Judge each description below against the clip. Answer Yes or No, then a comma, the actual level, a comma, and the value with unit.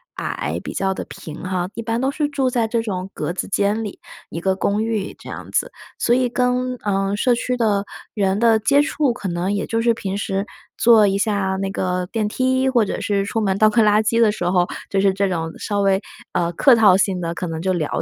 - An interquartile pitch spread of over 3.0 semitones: Yes, average, 3.4 semitones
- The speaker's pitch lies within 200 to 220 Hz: Yes, high, 205 Hz